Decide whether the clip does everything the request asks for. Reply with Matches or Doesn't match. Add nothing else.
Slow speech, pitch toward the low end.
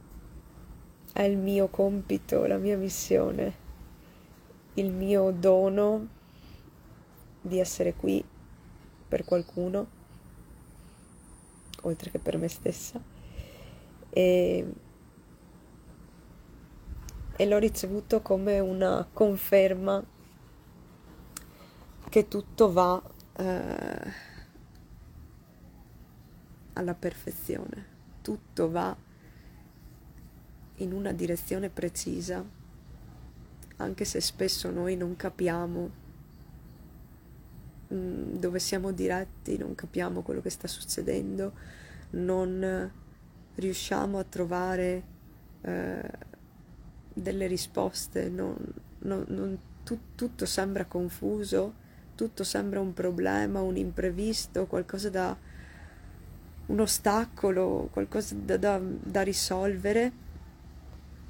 Doesn't match